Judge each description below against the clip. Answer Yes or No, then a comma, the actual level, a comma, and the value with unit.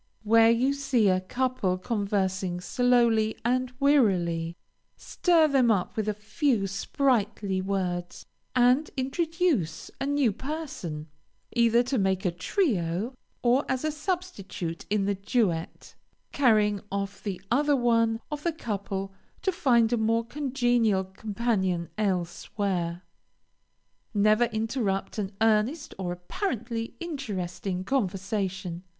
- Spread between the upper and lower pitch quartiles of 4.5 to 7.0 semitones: Yes, average, 5.0 semitones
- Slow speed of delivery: Yes, slow, 120 wpm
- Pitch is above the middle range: Yes, high, 220 Hz